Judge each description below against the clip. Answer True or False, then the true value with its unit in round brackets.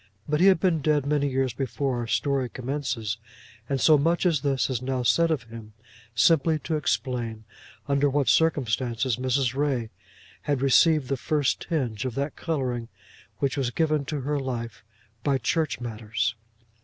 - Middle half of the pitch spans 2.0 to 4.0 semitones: True (3.6 semitones)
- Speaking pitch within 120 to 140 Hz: True (135 Hz)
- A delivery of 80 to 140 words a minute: False (165 wpm)